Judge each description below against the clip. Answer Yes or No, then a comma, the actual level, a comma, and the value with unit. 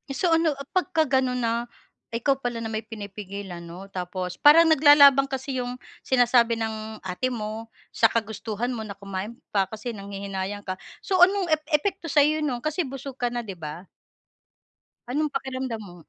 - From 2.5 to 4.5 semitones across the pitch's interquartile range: No, wide, 5.4 semitones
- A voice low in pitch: No, high, 235 Hz